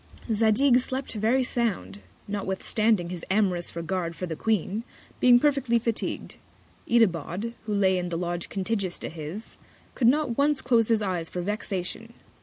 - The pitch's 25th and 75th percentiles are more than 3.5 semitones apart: Yes, average, 4.7 semitones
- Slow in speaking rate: No, average, 150 wpm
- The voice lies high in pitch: Yes, high, 210 Hz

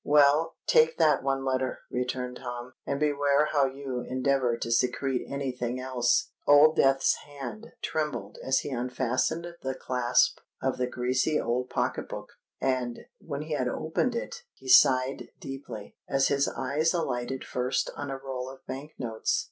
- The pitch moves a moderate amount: No, narrow, 2.2 semitones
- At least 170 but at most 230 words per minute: No, average, 155 wpm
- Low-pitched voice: Yes, low, 130 Hz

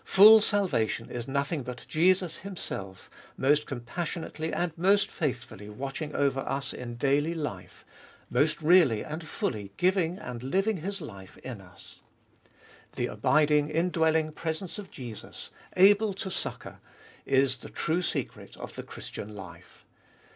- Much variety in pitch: Yes, wide, 6.0 semitones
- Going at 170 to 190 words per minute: No, slow, 135 wpm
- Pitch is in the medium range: Yes, medium, 150 Hz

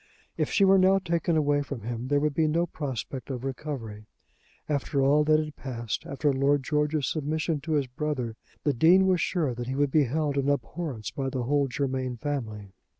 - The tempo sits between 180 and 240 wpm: Yes, average, 200 wpm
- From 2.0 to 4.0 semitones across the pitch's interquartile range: Yes, average, 3.0 semitones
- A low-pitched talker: No, medium, 145 Hz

